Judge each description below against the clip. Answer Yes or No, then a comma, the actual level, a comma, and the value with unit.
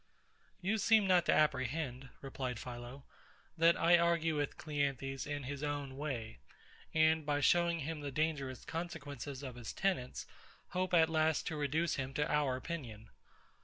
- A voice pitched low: No, medium, 145 Hz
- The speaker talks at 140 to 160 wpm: Yes, average, 155 wpm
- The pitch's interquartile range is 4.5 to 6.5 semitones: No, average, 3.4 semitones